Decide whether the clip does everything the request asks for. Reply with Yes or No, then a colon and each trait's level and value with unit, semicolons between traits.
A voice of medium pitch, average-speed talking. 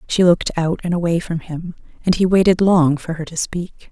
No: medium, 170 Hz; fast, 230 wpm